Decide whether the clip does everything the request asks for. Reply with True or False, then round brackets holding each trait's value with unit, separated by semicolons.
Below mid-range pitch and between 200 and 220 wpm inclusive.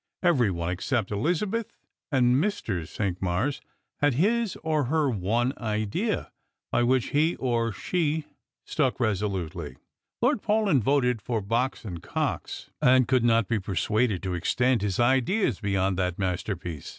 False (120 Hz; 140 wpm)